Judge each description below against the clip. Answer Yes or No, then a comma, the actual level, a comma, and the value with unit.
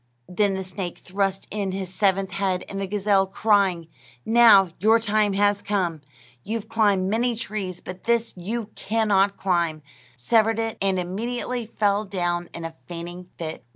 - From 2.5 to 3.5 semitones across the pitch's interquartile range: Yes, average, 2.8 semitones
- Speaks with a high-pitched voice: Yes, high, 195 Hz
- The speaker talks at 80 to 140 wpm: No, average, 160 wpm